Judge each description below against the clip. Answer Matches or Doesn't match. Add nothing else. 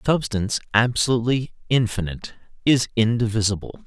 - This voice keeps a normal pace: Doesn't match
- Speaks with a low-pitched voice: Matches